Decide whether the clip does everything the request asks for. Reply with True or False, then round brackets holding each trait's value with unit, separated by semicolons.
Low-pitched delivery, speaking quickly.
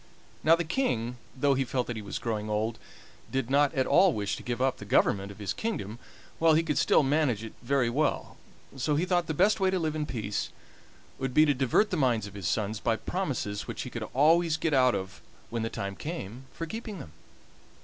True (130 Hz; 225 wpm)